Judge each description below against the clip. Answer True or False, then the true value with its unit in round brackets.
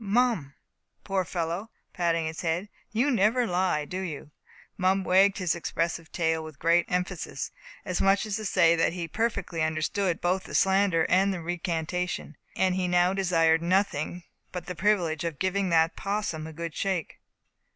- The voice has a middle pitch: True (180 Hz)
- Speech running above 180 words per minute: False (170 wpm)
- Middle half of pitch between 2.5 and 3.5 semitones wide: True (2.9 semitones)